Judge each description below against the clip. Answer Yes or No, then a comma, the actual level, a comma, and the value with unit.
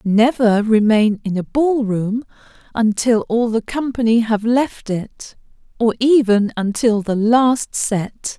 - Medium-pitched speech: No, high, 225 Hz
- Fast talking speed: No, slow, 135 wpm